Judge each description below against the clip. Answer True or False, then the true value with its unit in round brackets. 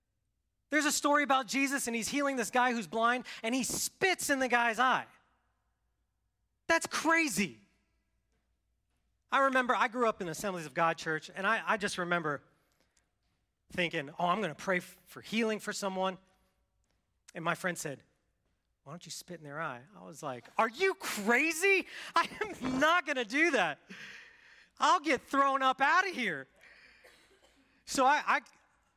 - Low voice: False (225 Hz)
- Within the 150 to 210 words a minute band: True (170 wpm)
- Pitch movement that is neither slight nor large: False (8.0 semitones)